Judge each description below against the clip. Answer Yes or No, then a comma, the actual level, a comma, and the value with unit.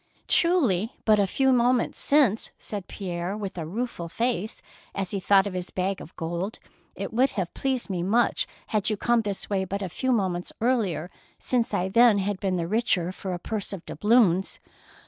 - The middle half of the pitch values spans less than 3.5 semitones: No, average, 4.3 semitones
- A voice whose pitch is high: Yes, high, 200 Hz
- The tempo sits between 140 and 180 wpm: No, average, 195 wpm